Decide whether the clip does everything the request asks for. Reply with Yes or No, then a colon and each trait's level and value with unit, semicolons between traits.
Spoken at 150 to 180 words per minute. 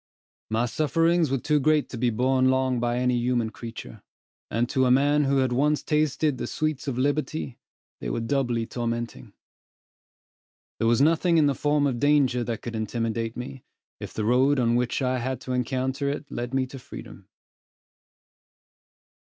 Yes: average, 170 wpm